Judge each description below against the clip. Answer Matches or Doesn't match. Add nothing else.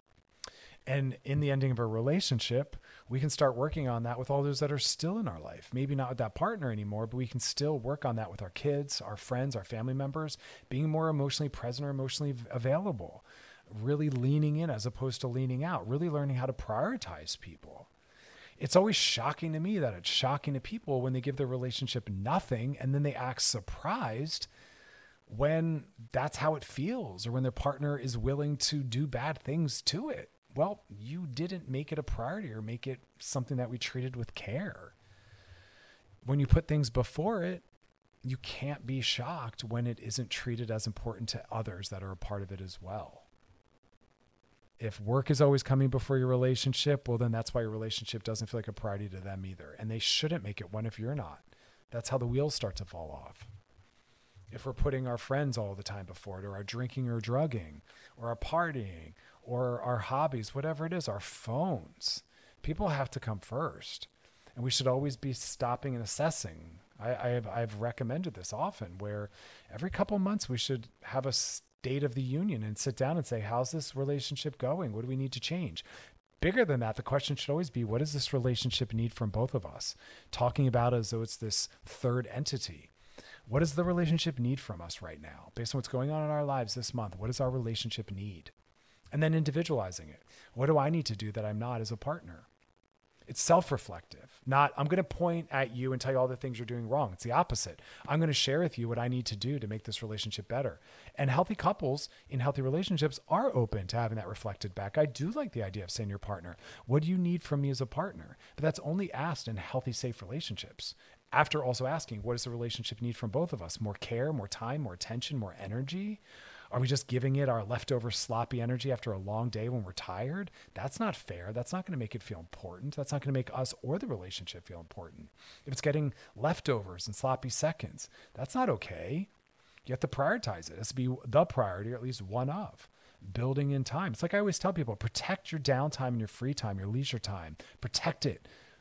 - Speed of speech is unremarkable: Doesn't match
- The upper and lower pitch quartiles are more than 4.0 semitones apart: Matches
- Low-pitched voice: Matches